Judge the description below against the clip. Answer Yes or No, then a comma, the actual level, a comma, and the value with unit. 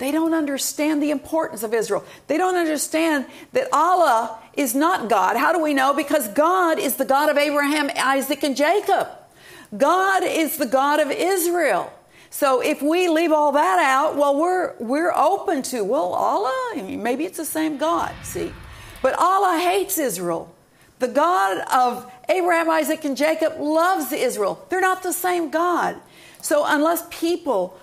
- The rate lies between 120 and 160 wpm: No, average, 170 wpm